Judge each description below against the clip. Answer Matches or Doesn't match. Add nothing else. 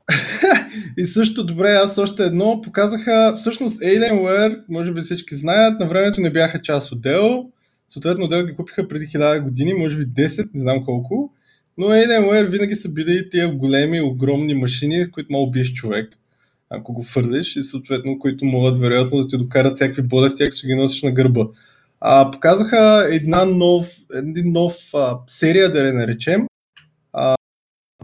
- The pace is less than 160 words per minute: Doesn't match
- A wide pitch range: Matches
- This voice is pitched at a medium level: Matches